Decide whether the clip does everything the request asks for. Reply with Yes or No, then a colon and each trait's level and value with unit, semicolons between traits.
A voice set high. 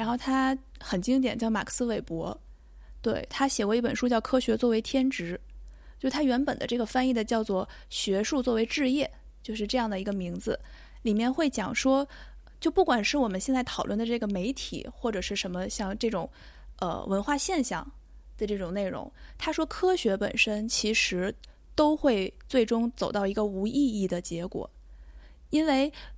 Yes: high, 230 Hz